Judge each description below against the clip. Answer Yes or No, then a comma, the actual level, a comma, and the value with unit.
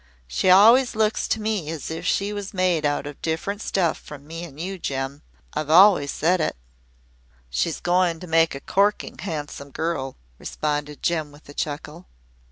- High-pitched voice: No, medium, 165 Hz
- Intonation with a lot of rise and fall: No, average, 4.3 semitones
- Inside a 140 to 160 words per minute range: No, average, 175 wpm